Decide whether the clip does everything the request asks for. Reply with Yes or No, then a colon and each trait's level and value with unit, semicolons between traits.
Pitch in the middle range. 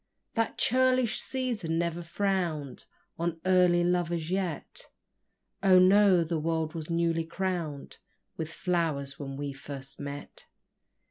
Yes: medium, 170 Hz